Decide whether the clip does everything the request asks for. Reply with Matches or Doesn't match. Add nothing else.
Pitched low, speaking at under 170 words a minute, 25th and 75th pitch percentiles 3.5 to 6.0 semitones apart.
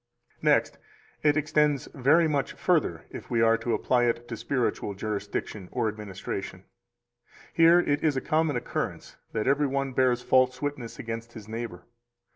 Matches